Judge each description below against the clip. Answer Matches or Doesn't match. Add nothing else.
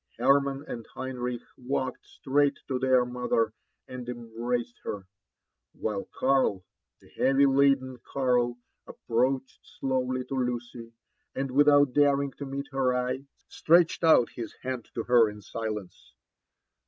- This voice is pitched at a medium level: Doesn't match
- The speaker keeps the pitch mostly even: Matches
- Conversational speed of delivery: Doesn't match